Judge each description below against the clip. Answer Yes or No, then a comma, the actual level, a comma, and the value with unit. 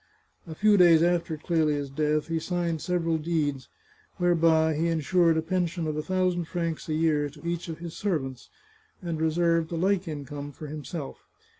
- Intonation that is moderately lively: No, narrow, 2.1 semitones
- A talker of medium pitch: Yes, medium, 165 Hz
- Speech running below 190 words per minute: Yes, average, 170 wpm